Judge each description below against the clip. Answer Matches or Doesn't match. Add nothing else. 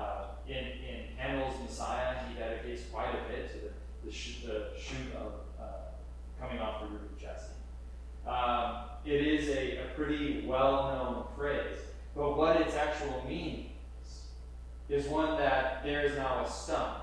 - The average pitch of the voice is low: Matches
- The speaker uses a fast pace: Doesn't match